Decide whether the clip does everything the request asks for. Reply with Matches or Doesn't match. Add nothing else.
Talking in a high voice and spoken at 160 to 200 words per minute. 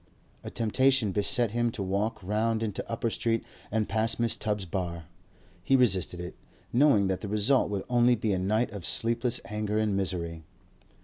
Doesn't match